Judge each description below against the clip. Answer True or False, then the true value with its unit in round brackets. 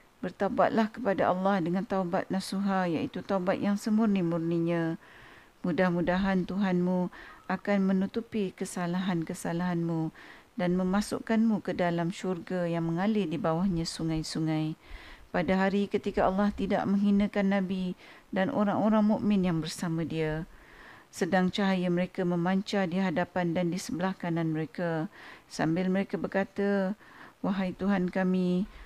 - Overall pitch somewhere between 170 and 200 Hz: True (185 Hz)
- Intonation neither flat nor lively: False (2.2 semitones)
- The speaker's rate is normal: True (115 wpm)